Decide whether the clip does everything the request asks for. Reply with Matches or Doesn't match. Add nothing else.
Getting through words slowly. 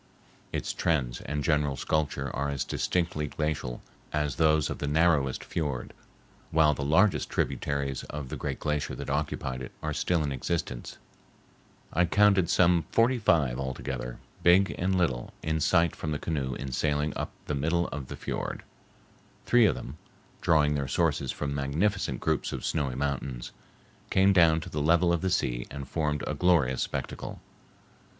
Doesn't match